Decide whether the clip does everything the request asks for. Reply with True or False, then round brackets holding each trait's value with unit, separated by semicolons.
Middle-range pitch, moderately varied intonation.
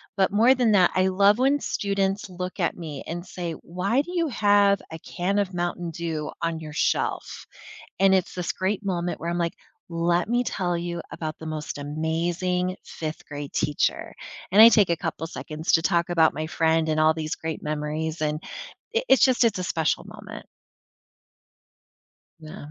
True (175 Hz; 3.4 semitones)